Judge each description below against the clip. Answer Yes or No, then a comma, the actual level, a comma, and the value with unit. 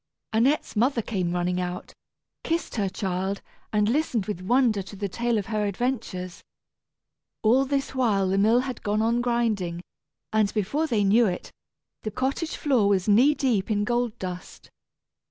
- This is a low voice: No, high, 215 Hz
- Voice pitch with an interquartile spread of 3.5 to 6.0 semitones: Yes, average, 4.0 semitones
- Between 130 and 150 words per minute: No, average, 160 wpm